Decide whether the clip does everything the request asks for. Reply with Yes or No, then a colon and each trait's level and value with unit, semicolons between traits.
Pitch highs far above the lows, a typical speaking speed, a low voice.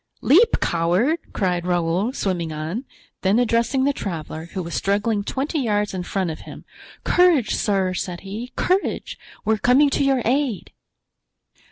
No: wide, 6.6 semitones; average, 155 wpm; high, 205 Hz